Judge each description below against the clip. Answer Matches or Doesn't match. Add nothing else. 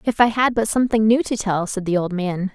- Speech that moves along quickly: Matches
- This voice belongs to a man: Doesn't match